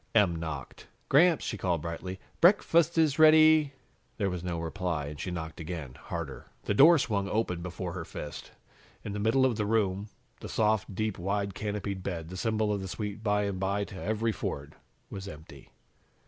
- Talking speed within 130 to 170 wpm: No, average, 190 wpm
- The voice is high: No, low, 100 Hz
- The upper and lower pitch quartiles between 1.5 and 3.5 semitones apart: No, average, 4.0 semitones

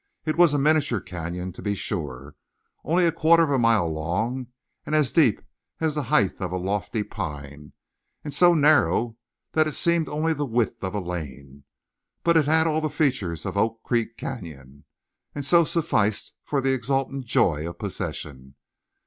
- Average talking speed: Yes, average, 175 wpm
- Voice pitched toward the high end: No, low, 115 Hz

